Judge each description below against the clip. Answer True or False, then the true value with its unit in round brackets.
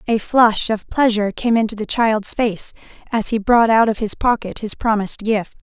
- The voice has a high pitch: True (220 Hz)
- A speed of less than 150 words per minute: False (200 wpm)